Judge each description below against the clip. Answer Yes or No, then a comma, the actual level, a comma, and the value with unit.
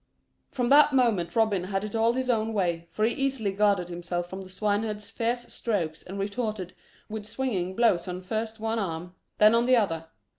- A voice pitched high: Yes, high, 210 Hz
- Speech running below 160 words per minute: No, average, 190 wpm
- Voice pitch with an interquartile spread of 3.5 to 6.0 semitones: Yes, average, 3.9 semitones